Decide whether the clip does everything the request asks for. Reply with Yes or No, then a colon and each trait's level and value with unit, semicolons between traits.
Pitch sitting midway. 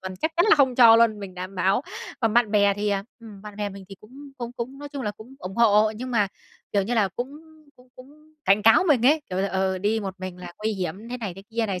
No: high, 215 Hz